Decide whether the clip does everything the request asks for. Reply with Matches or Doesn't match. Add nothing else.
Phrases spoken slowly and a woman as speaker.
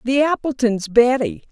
Matches